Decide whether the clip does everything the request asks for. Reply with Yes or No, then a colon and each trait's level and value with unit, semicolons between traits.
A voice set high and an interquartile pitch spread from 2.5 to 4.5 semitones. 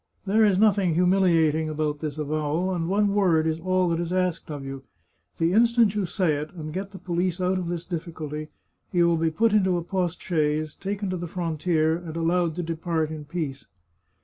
No: medium, 170 Hz; average, 2.8 semitones